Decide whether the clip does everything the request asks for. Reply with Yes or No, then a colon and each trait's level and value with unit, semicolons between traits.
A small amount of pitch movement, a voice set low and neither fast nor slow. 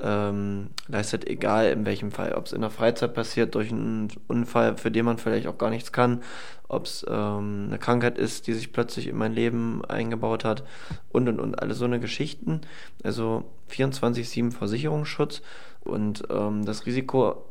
Yes: narrow, 1.9 semitones; low, 115 Hz; average, 170 wpm